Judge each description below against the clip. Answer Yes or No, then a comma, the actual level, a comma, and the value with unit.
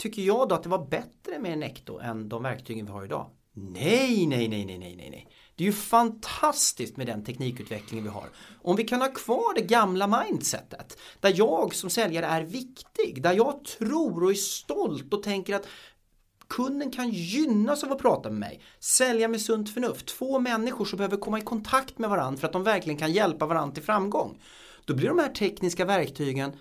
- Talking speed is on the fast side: Yes, fast, 200 wpm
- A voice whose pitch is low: No, high, 200 Hz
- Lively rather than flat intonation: Yes, wide, 7.9 semitones